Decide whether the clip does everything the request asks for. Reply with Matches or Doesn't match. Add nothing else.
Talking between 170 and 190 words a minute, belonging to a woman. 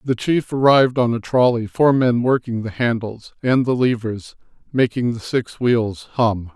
Doesn't match